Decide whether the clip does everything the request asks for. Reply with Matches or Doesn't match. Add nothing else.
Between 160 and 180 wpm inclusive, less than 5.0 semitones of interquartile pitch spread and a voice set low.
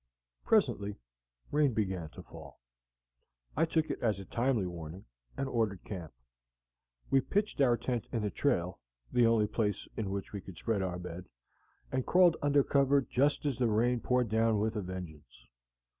Doesn't match